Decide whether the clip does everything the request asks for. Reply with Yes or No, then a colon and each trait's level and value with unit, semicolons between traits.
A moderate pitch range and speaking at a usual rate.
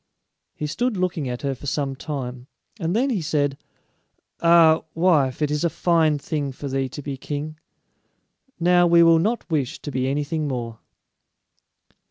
Yes: average, 3.6 semitones; average, 165 wpm